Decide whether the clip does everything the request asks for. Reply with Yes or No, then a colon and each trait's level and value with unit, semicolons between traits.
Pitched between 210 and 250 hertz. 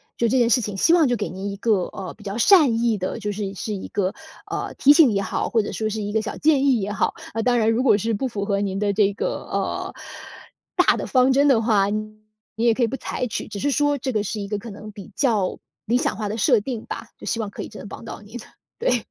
Yes: high, 215 Hz